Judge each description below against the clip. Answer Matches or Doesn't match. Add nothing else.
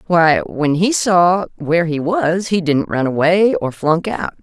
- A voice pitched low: Doesn't match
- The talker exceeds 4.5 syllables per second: Doesn't match